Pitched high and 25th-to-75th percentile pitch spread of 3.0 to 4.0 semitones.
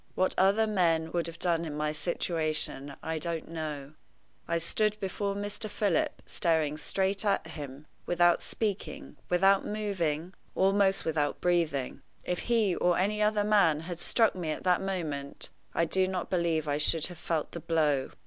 No: medium, 170 Hz; average, 3.6 semitones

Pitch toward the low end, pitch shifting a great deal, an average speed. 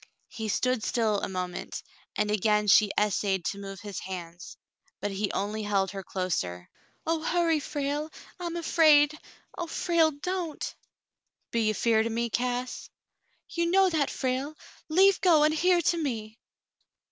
No: high, 240 Hz; wide, 7.5 semitones; average, 160 wpm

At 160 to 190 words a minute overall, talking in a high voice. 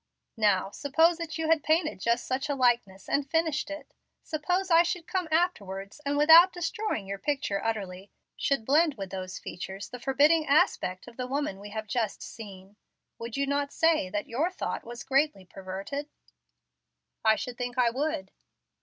Yes: average, 170 wpm; very high, 270 Hz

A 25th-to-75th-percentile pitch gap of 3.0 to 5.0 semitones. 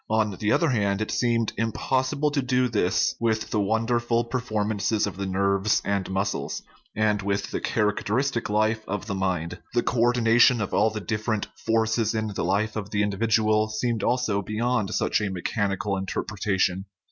No: narrow, 2.5 semitones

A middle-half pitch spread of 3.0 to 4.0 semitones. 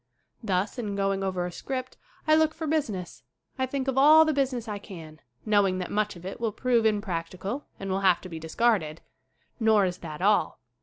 No: wide, 5.5 semitones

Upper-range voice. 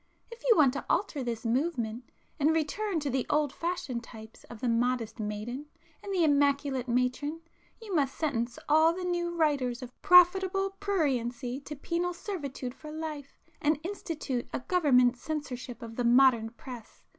Yes: very high, 280 Hz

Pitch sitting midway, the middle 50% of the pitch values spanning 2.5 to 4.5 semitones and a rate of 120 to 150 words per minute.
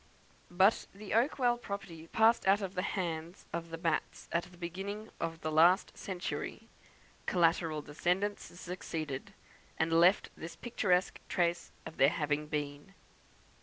Yes: medium, 175 Hz; average, 3.1 semitones; slow, 135 wpm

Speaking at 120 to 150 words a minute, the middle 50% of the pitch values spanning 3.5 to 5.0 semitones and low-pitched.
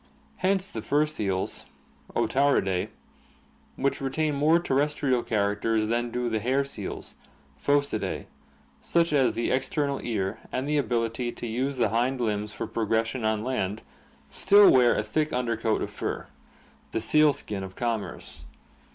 Yes: average, 145 wpm; average, 4.4 semitones; low, 120 Hz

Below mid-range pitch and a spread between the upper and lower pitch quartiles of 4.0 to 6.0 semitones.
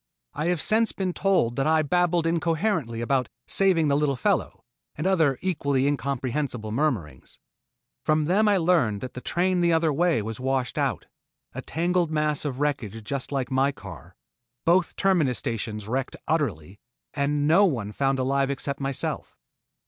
No: medium, 145 Hz; average, 4.7 semitones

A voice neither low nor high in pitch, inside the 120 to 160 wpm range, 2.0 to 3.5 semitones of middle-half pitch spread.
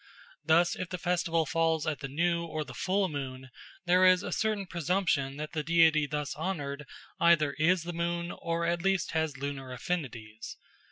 No: medium, 165 Hz; average, 175 wpm; average, 3.2 semitones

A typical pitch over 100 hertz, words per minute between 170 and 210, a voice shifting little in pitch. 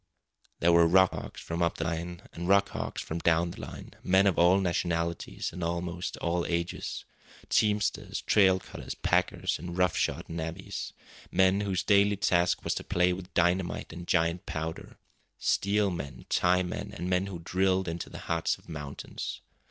No: very low, 90 Hz; average, 175 wpm; narrow, 1.9 semitones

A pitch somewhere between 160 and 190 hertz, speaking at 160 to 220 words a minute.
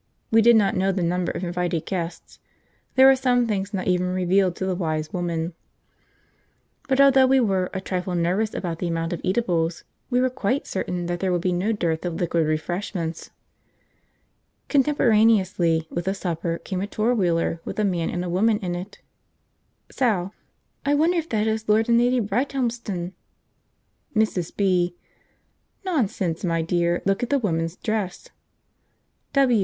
Yes: medium, 185 Hz; average, 165 wpm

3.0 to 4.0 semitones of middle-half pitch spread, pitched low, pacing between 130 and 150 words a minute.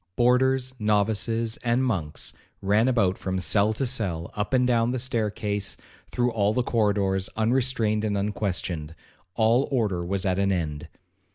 Yes: average, 3.6 semitones; low, 105 Hz; average, 145 wpm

